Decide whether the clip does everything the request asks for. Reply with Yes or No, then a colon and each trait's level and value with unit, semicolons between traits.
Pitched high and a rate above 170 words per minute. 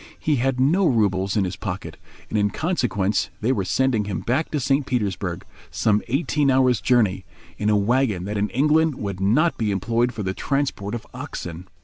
No: low, 115 Hz; average, 180 wpm